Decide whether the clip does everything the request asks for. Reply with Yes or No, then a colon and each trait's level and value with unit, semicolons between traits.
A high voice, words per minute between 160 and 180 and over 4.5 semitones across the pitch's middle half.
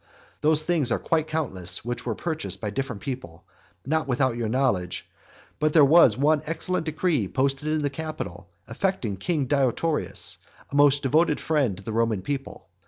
No: medium, 140 Hz; average, 170 wpm; average, 5.0 semitones